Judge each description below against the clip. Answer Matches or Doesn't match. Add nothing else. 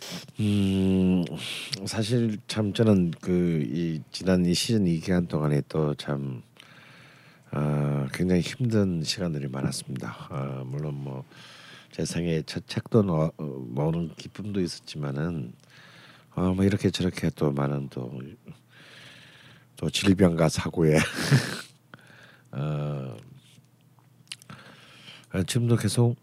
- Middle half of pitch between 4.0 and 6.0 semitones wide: Matches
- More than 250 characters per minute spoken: Doesn't match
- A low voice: Matches